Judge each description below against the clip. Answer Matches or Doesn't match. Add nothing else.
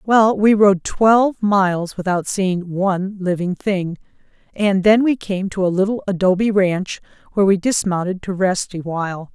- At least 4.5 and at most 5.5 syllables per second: Matches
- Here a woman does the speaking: Matches